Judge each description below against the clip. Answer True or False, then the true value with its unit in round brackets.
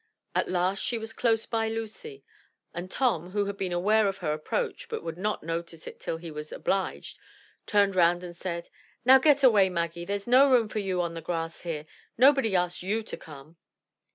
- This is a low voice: False (190 Hz)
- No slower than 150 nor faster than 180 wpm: False (205 wpm)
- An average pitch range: True (4.6 semitones)